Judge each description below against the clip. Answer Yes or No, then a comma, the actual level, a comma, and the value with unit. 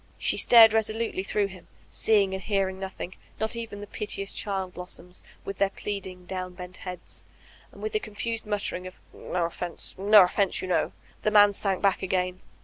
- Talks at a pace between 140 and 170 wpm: No, average, 185 wpm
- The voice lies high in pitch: Yes, high, 195 Hz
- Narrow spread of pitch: Yes, narrow, 2.3 semitones